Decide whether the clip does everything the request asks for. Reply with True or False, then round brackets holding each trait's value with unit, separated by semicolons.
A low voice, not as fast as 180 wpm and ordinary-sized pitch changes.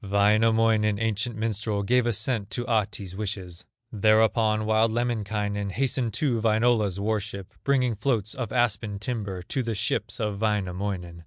False (110 Hz; 140 wpm; 2.1 semitones)